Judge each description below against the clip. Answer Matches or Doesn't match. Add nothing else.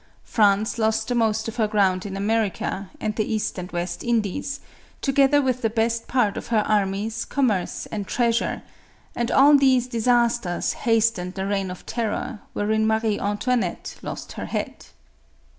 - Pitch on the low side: Doesn't match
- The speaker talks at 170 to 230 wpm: Doesn't match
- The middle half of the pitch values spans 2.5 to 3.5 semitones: Matches